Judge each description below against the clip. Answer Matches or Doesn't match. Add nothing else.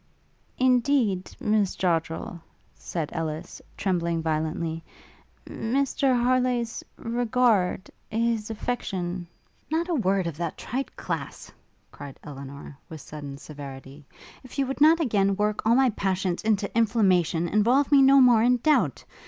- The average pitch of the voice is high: Matches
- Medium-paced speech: Doesn't match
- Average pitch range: Doesn't match